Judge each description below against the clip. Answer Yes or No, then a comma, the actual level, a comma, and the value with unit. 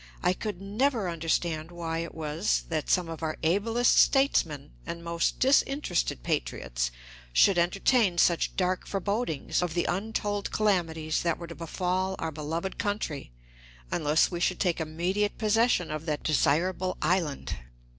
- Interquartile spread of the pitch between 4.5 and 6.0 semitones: No, average, 3.8 semitones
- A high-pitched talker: No, medium, 175 Hz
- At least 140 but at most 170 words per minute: Yes, average, 145 wpm